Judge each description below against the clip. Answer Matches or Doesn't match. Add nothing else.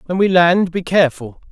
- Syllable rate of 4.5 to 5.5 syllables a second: Matches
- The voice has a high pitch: Doesn't match